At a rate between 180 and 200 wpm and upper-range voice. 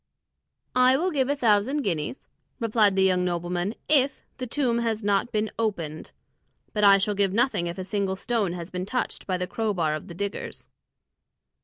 Yes: average, 185 wpm; high, 205 Hz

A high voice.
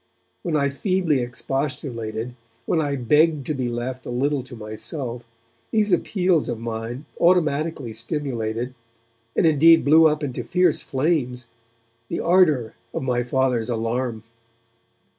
No: low, 135 Hz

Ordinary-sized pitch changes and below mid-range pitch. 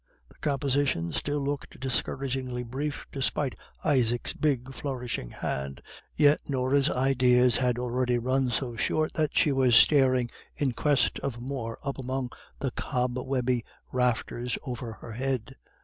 No: narrow, 2.1 semitones; low, 130 Hz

